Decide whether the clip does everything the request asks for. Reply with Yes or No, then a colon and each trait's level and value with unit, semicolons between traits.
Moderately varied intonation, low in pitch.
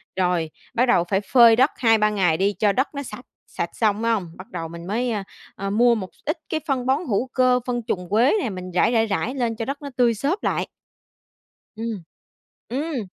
No: average, 4.1 semitones; high, 225 Hz